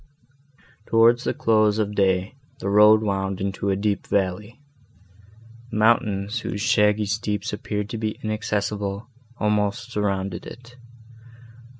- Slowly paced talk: Yes, slow, 115 wpm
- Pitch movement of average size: No, narrow, 1.6 semitones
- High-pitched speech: No, low, 105 Hz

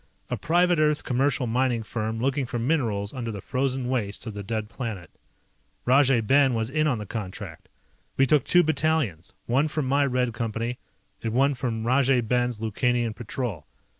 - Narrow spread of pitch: No, average, 3.4 semitones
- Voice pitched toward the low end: Yes, low, 125 Hz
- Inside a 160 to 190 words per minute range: Yes, average, 170 wpm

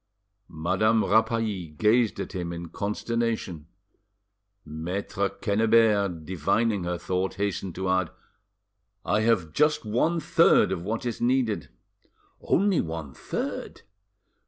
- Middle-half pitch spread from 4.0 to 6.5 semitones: Yes, average, 4.6 semitones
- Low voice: Yes, low, 100 Hz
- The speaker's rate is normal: No, slow, 110 wpm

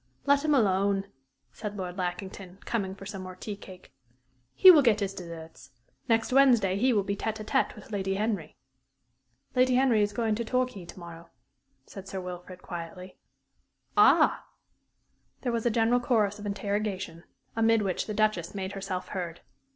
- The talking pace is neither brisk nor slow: Yes, average, 165 wpm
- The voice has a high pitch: Yes, high, 200 Hz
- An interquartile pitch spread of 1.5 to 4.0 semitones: Yes, average, 3.3 semitones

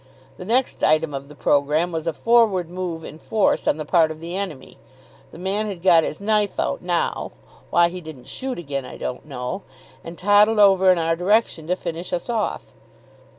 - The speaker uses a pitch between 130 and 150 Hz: No, medium, 175 Hz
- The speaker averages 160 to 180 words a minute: No, average, 195 wpm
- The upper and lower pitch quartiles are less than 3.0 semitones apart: No, average, 4.0 semitones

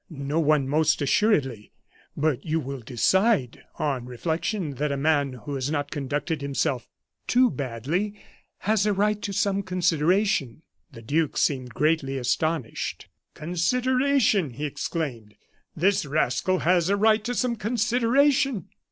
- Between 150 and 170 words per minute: No, slow, 135 wpm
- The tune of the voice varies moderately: No, wide, 6.7 semitones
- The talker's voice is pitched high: No, medium, 160 Hz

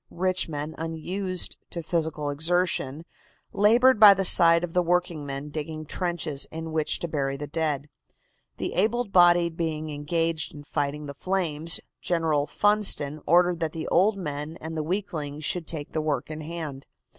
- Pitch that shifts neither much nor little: Yes, average, 3.0 semitones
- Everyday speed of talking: Yes, average, 160 wpm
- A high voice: No, medium, 160 Hz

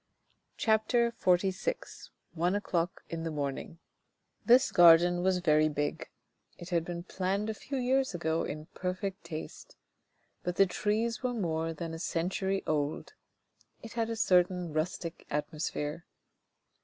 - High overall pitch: No, medium, 175 Hz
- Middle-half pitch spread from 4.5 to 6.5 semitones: No, average, 3.9 semitones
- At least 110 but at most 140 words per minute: Yes, slow, 135 wpm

